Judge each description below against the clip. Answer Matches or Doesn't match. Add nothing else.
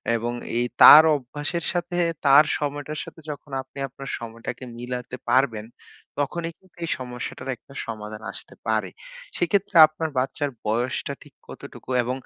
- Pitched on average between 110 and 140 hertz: Matches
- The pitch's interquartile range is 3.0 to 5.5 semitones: Matches